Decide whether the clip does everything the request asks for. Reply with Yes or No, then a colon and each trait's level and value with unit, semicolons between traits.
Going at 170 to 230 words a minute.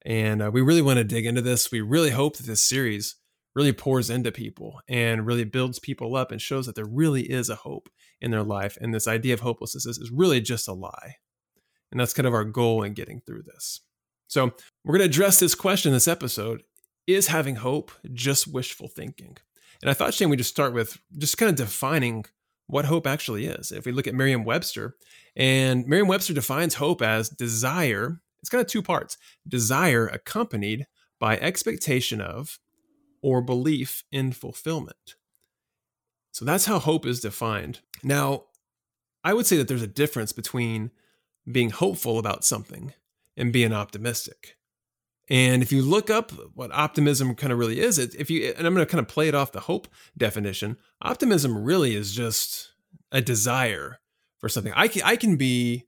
Yes: average, 185 wpm